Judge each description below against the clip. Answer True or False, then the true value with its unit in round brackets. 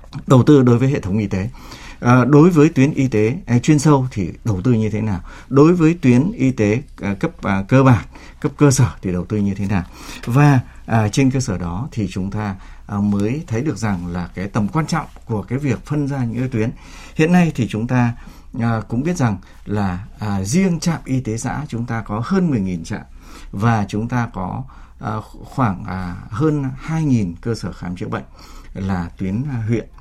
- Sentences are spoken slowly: False (195 wpm)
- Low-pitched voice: True (115 Hz)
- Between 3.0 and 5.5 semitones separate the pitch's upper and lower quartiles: True (5.1 semitones)